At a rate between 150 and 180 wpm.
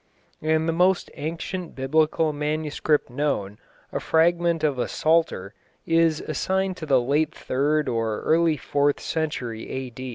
No: slow, 135 wpm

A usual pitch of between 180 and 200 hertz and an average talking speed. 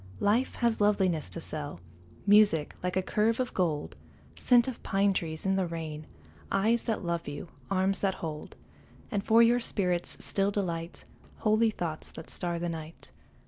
Yes: high, 190 Hz; average, 165 wpm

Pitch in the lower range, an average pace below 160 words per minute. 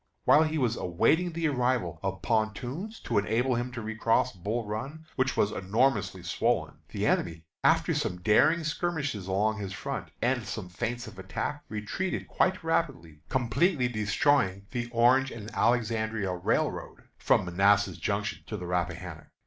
Yes: low, 115 Hz; average, 150 wpm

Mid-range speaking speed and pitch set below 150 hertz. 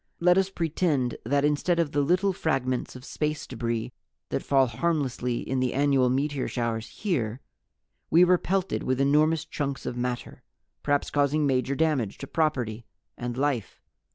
Yes: average, 155 wpm; medium, 140 Hz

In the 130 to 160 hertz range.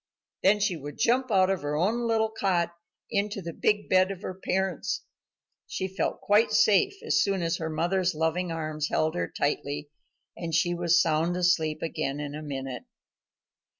No: medium, 175 Hz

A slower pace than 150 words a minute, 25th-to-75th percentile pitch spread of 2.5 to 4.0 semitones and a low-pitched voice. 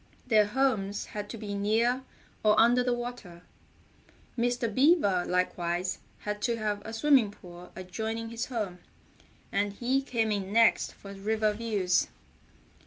No: average, 140 wpm; average, 3.1 semitones; high, 215 Hz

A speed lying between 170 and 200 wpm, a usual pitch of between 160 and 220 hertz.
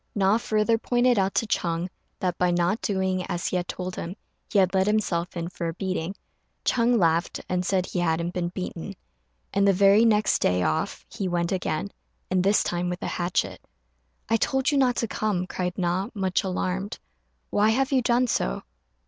Yes: average, 190 wpm; medium, 185 Hz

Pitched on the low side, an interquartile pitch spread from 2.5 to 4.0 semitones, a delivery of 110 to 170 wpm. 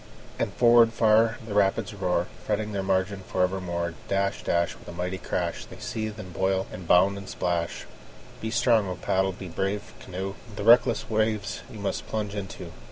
No: low, 100 Hz; average, 2.8 semitones; average, 180 wpm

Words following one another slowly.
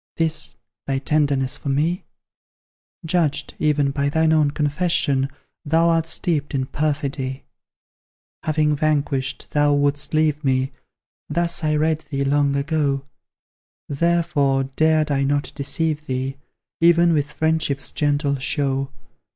Yes: slow, 120 wpm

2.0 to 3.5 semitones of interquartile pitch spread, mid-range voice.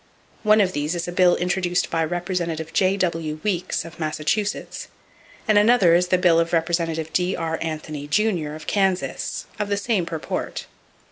Yes: average, 2.8 semitones; medium, 175 Hz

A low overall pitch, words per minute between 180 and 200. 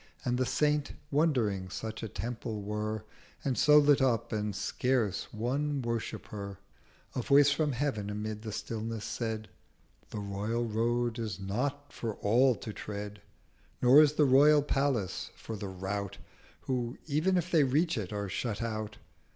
No: low, 115 Hz; average, 160 wpm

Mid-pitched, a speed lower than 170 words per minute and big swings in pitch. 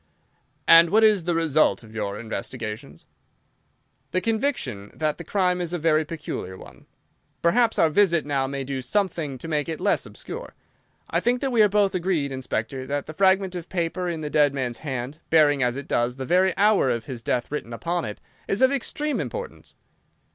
No: medium, 160 Hz; average, 190 wpm; wide, 6.1 semitones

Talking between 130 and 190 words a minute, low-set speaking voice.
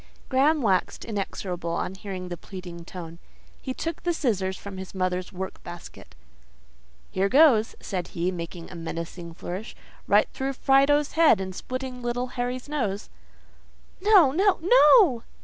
No: average, 145 wpm; high, 205 Hz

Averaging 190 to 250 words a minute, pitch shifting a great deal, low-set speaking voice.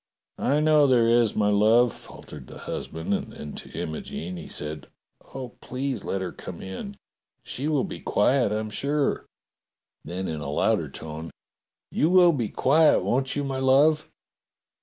No: average, 160 wpm; wide, 7.2 semitones; low, 120 Hz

